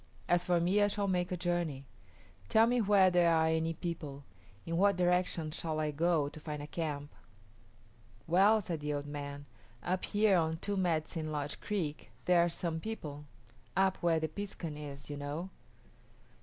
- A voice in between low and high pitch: Yes, medium, 165 Hz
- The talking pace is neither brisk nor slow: Yes, average, 175 wpm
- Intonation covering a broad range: No, average, 3.3 semitones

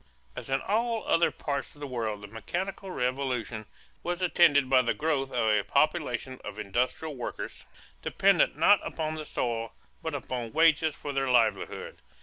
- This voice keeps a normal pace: Yes, average, 160 wpm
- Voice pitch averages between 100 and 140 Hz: Yes, low, 135 Hz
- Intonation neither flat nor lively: Yes, average, 4.8 semitones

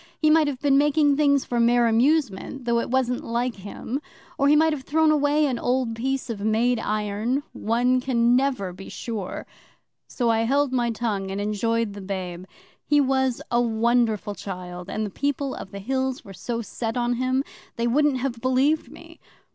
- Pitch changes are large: No, average, 3.6 semitones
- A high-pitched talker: Yes, high, 240 Hz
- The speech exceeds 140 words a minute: Yes, average, 185 wpm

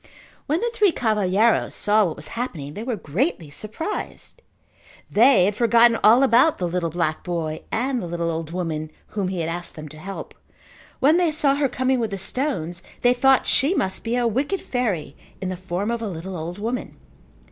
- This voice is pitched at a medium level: No, high, 210 Hz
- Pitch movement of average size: No, wide, 6.5 semitones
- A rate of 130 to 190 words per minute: No, average, 200 wpm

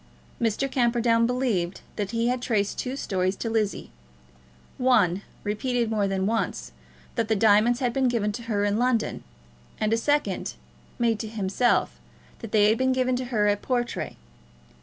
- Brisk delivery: No, average, 165 wpm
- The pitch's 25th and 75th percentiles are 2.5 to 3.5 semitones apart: Yes, average, 3.1 semitones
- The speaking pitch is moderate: No, high, 230 Hz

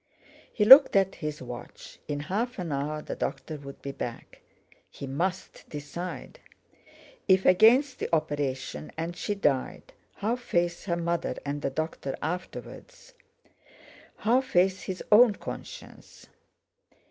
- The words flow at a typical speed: No, slow, 130 wpm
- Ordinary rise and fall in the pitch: No, wide, 6.1 semitones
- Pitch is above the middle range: No, medium, 170 Hz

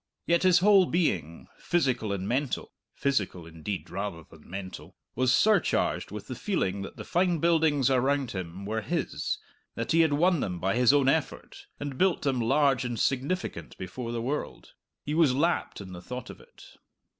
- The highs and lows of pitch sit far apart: Yes, wide, 8.1 semitones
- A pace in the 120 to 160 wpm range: No, average, 180 wpm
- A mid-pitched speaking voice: No, low, 130 Hz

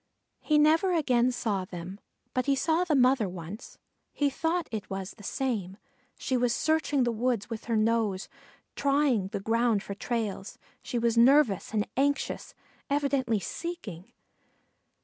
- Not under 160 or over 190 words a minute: No, average, 150 wpm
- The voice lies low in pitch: No, high, 235 Hz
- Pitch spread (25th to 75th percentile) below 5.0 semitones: No, wide, 5.4 semitones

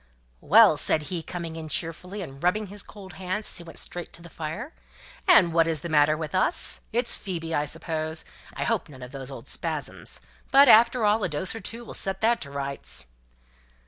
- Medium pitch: Yes, medium, 170 Hz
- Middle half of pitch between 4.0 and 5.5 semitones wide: Yes, average, 5.0 semitones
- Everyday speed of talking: No, fast, 210 wpm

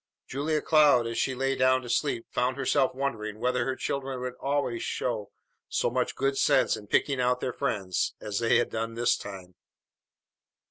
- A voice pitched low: Yes, low, 125 Hz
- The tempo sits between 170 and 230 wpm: Yes, average, 180 wpm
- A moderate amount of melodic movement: Yes, average, 3.0 semitones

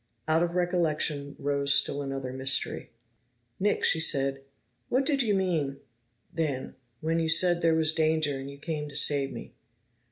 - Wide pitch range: No, average, 3.2 semitones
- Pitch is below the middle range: No, medium, 155 Hz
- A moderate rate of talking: Yes, average, 160 wpm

